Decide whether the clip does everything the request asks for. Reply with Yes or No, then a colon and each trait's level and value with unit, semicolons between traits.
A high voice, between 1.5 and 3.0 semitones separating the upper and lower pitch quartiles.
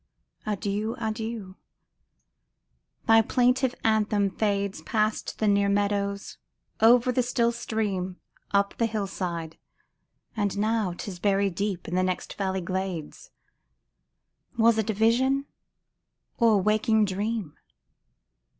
Yes: high, 205 Hz; narrow, 2.5 semitones